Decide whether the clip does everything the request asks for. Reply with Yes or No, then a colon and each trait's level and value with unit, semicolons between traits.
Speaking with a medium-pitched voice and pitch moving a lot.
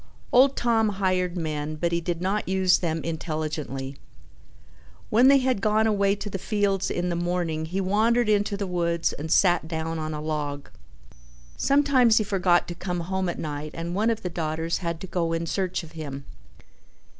No: medium, 175 Hz; average, 4.0 semitones